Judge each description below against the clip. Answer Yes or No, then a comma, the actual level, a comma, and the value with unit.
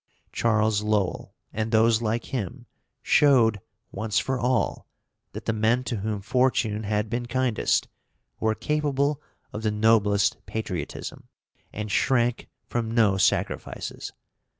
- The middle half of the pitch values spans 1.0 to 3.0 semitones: Yes, narrow, 2.6 semitones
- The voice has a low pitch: Yes, low, 110 Hz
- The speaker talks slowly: Yes, slow, 125 wpm